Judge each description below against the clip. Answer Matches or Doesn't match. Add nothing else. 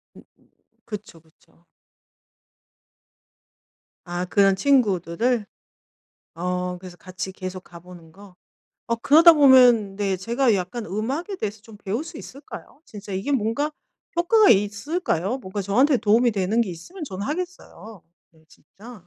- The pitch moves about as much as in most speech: Doesn't match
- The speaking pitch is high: Matches